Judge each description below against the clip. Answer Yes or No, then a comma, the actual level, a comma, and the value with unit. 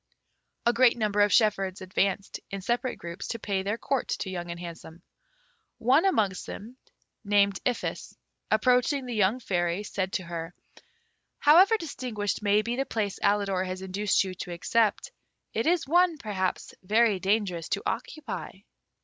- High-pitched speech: Yes, high, 205 Hz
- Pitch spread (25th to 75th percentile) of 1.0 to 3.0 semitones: No, average, 4.2 semitones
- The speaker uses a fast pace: No, average, 155 wpm